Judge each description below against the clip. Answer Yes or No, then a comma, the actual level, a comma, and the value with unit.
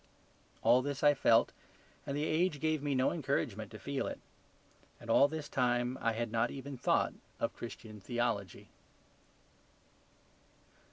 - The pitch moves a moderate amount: Yes, average, 3.7 semitones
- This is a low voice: Yes, low, 130 Hz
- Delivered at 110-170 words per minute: Yes, average, 145 wpm